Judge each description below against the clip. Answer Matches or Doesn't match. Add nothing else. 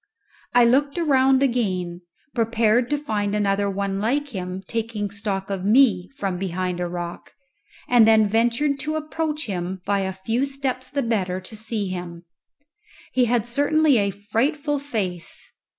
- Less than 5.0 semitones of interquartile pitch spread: Doesn't match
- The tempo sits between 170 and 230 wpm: Doesn't match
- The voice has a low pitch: Doesn't match